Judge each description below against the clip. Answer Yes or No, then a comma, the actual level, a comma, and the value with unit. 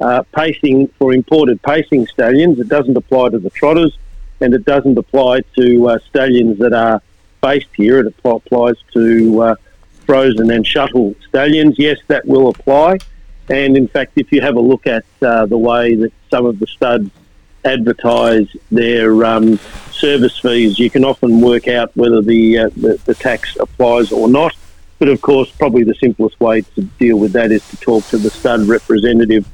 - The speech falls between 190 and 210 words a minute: No, average, 180 wpm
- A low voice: Yes, low, 120 Hz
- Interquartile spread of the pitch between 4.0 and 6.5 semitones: No, average, 2.9 semitones